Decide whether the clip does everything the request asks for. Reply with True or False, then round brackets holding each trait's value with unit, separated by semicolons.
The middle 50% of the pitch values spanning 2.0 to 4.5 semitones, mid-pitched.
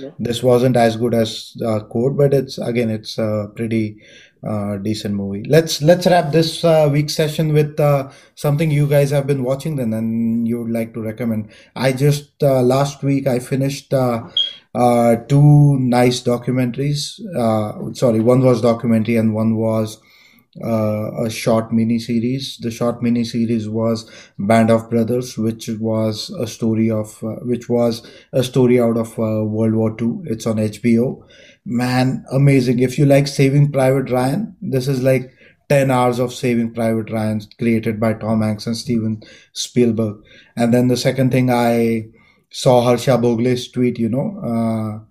False (2.9 semitones; 120 Hz)